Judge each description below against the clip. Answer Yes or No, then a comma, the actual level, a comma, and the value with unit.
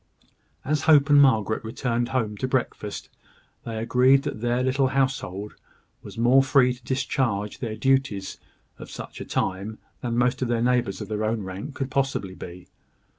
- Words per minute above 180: No, average, 170 wpm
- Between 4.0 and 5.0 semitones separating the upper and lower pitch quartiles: No, average, 3.6 semitones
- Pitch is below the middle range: Yes, low, 120 Hz